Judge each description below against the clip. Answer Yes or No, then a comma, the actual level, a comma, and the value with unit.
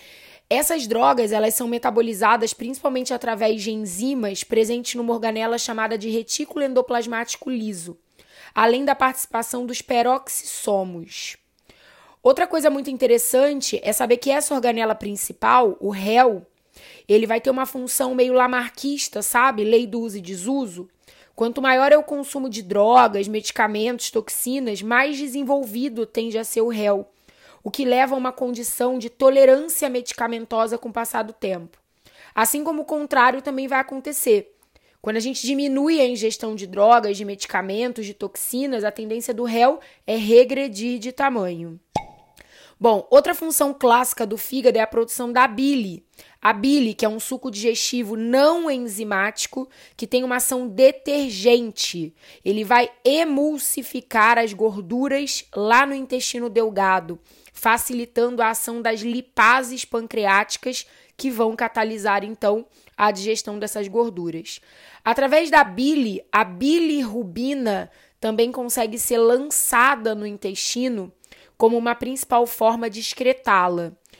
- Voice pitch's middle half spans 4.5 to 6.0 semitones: No, average, 3.1 semitones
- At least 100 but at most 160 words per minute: Yes, average, 135 wpm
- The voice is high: Yes, high, 235 Hz